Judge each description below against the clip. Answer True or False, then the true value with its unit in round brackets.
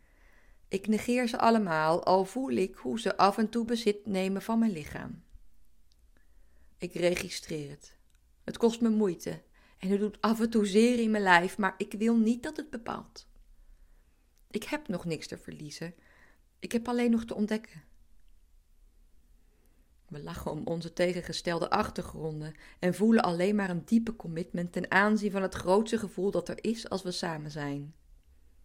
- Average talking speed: True (165 wpm)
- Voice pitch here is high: False (180 Hz)